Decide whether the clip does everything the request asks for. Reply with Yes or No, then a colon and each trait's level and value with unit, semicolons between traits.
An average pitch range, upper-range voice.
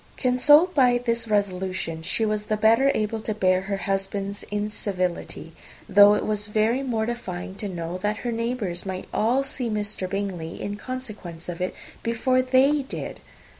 Yes: average, 4.0 semitones; high, 210 Hz